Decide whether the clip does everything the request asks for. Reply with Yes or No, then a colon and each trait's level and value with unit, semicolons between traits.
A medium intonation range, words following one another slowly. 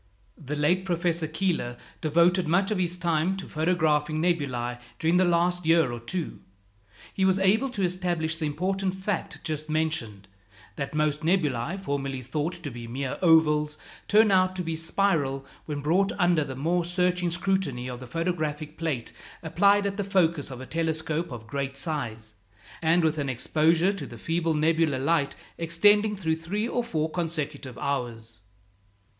No: average, 3.8 semitones; average, 160 wpm